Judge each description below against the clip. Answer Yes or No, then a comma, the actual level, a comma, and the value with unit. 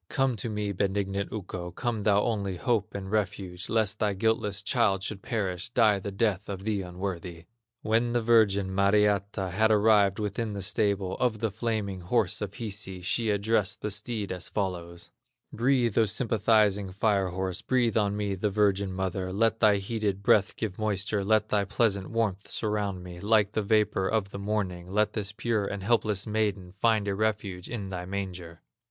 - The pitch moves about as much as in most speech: No, narrow, 2.2 semitones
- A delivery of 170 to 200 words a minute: Yes, average, 175 wpm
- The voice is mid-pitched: No, low, 100 Hz